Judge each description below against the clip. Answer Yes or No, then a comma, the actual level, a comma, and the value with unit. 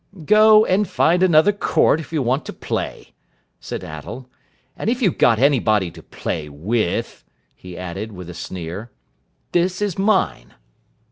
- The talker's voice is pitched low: Yes, low, 130 Hz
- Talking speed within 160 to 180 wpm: No, average, 150 wpm